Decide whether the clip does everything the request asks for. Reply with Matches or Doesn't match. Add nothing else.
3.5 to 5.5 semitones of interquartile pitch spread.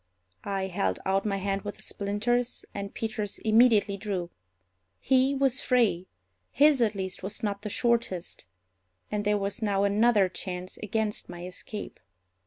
Doesn't match